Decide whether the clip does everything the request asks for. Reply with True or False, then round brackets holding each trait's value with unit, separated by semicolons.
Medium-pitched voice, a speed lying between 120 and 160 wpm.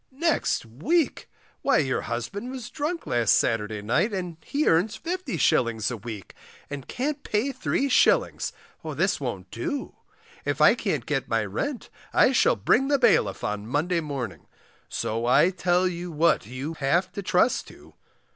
True (175 Hz; 155 wpm)